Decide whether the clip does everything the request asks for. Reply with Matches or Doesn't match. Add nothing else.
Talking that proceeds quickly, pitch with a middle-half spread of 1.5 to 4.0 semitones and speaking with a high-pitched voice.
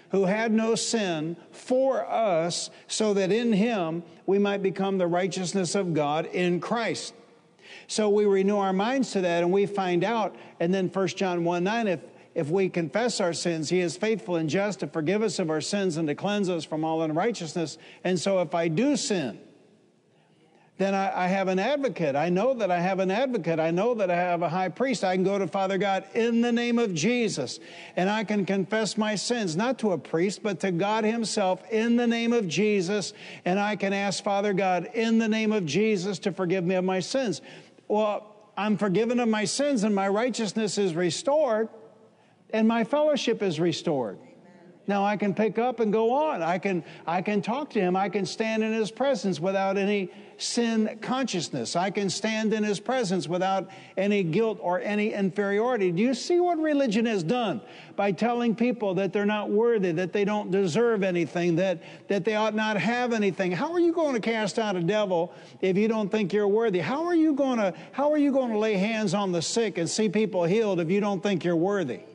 Matches